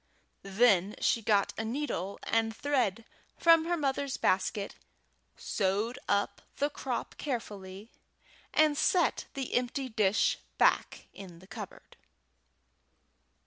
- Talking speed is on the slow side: Yes, slow, 110 wpm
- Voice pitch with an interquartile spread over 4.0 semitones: Yes, wide, 5.5 semitones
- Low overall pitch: No, high, 225 Hz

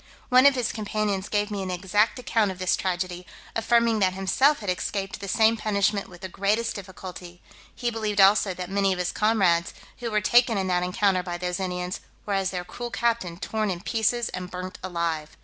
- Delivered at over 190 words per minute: Yes, average, 200 wpm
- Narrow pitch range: No, average, 3.2 semitones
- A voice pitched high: Yes, high, 195 Hz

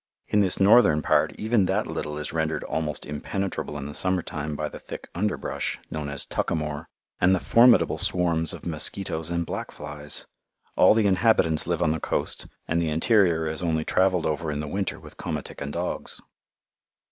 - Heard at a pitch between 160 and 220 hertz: No, very low, 80 Hz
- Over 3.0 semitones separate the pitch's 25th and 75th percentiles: Yes, average, 3.6 semitones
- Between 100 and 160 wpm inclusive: No, average, 185 wpm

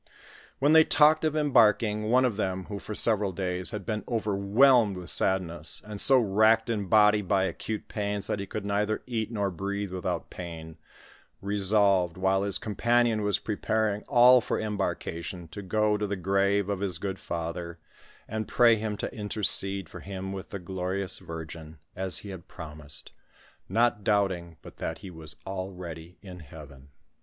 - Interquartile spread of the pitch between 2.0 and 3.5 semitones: Yes, average, 2.9 semitones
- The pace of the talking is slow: No, average, 170 wpm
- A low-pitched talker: Yes, low, 100 Hz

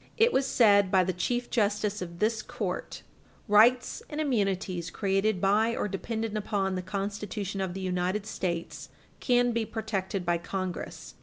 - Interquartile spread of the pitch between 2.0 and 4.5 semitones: Yes, average, 2.9 semitones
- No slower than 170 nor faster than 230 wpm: No, average, 160 wpm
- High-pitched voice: Yes, high, 200 Hz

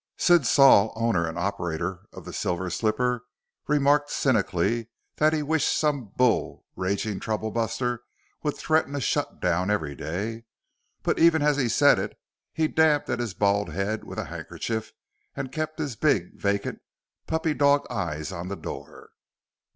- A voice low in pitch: Yes, low, 115 Hz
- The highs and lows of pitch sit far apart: Yes, wide, 6.8 semitones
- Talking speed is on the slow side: No, average, 155 wpm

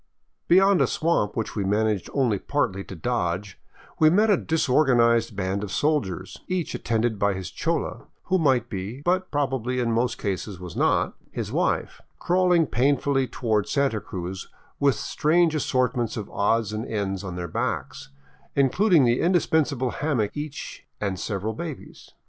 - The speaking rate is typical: Yes, average, 155 wpm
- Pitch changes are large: Yes, wide, 6.4 semitones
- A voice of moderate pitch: No, low, 120 Hz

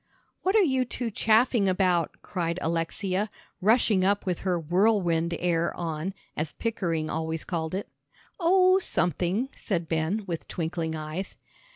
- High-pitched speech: No, medium, 180 Hz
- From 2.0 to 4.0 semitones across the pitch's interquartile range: No, average, 4.6 semitones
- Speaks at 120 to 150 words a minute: Yes, average, 140 wpm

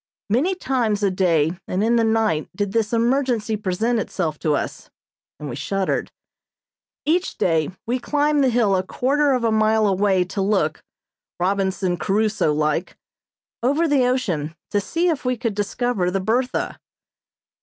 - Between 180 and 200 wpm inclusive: No, average, 155 wpm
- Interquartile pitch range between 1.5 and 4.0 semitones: No, average, 5.0 semitones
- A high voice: Yes, high, 215 Hz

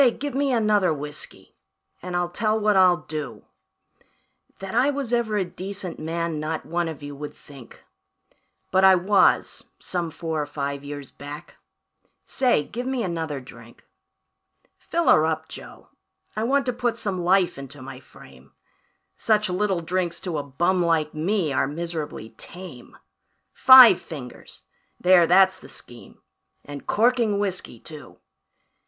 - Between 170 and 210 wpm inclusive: No, average, 150 wpm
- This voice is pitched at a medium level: Yes, medium, 175 Hz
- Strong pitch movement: Yes, wide, 5.8 semitones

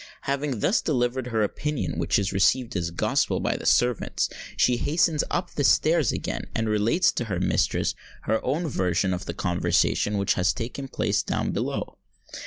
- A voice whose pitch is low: Yes, low, 120 Hz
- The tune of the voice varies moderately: No, wide, 6.0 semitones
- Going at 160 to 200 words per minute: Yes, average, 170 wpm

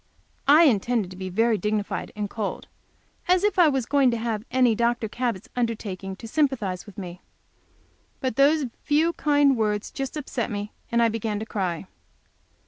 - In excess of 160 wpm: Yes, average, 170 wpm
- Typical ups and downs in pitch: Yes, average, 4.7 semitones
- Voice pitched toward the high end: Yes, high, 230 Hz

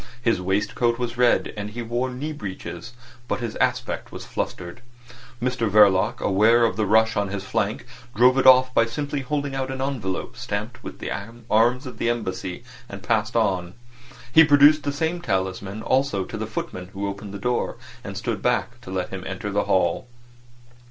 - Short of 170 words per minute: No, average, 185 wpm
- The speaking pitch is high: No, low, 115 Hz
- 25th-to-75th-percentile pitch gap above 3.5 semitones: Yes, average, 4.2 semitones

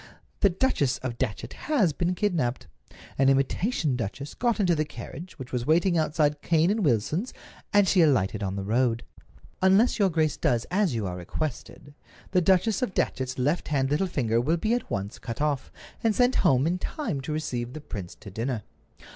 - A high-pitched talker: No, medium, 150 Hz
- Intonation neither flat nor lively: No, wide, 7.0 semitones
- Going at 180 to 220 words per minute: Yes, average, 190 wpm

